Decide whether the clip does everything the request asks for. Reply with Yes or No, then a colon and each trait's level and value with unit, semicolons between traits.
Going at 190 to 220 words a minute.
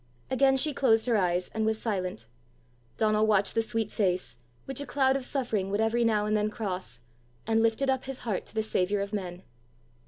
Yes: average, 200 wpm